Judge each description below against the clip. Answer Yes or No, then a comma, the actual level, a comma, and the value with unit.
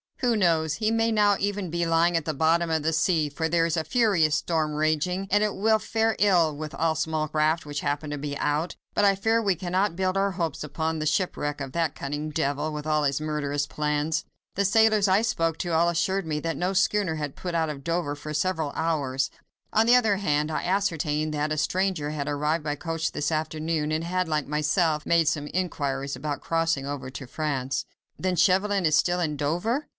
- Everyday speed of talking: No, fast, 220 wpm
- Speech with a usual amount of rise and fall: Yes, average, 3.6 semitones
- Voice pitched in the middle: Yes, medium, 160 Hz